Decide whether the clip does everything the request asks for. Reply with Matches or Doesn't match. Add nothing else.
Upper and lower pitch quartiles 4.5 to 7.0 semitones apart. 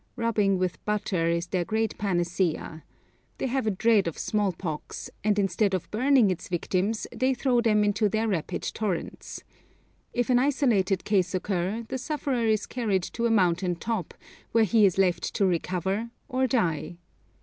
Doesn't match